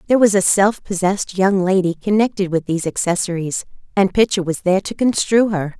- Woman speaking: Yes, female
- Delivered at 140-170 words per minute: No, average, 185 wpm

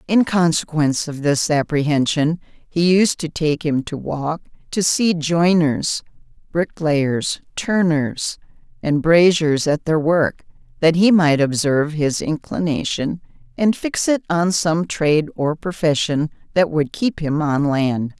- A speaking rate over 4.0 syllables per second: No, 3.9 syllables/s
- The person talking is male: No, female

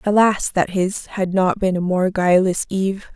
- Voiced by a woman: Yes, female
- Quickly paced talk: No, average, 190 wpm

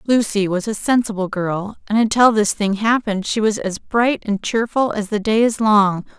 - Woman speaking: Yes, female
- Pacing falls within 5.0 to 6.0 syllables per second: No, 4.8 syllables/s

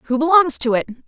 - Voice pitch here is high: Yes, very high, 285 Hz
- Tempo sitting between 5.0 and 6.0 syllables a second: Yes, 5.7 syllables/s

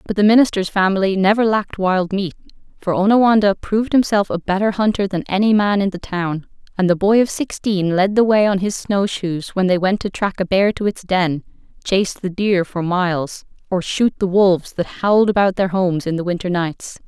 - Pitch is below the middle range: No, high, 195 Hz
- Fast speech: Yes, fast, 215 wpm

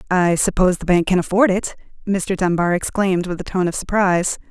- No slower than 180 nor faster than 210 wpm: Yes, average, 200 wpm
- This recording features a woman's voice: Yes, female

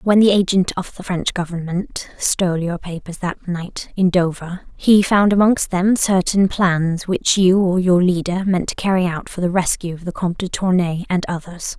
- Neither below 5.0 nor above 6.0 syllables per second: No, 4.7 syllables/s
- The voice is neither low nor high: Yes, medium, 180 Hz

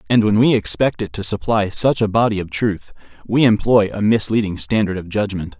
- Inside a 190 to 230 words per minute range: Yes, fast, 205 wpm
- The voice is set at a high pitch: No, low, 110 Hz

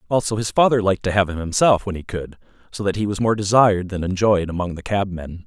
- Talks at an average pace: No, fast, 240 wpm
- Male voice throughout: Yes, male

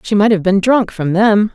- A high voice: Yes, high, 205 Hz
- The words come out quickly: Yes, fast, 270 wpm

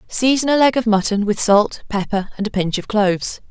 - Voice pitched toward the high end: Yes, high, 215 Hz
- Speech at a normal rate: No, fast, 225 wpm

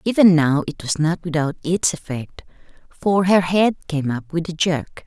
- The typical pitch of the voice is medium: Yes, medium, 165 Hz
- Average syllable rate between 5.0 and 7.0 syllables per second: No, 4.4 syllables/s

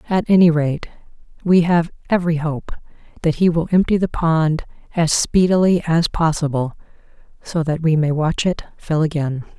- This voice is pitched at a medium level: Yes, medium, 165 Hz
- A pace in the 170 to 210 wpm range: No, average, 155 wpm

